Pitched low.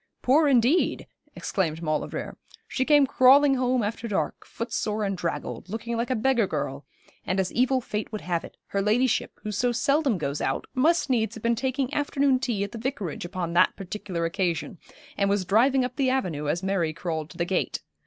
No: high, 220 Hz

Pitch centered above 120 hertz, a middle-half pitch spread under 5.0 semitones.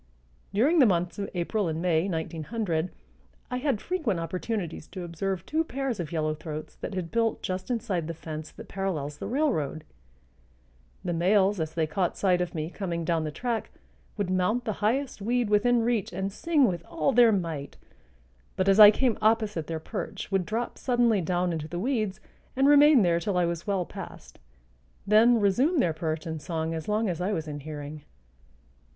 No: high, 190 Hz; wide, 5.4 semitones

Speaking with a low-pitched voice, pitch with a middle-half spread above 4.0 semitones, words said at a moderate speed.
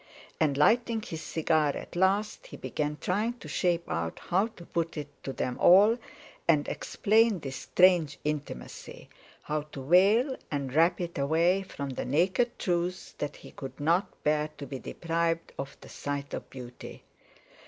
No: medium, 165 Hz; average, 4.6 semitones; average, 160 wpm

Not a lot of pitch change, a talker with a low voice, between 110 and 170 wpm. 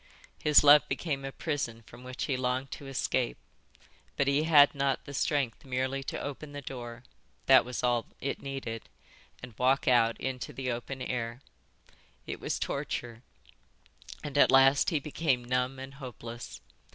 Yes: narrow, 2.1 semitones; low, 130 Hz; average, 150 wpm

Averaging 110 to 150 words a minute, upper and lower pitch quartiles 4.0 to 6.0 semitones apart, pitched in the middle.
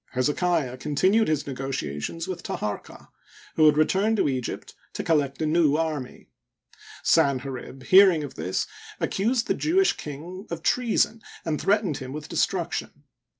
Yes: average, 145 wpm; wide, 5.5 semitones; medium, 155 Hz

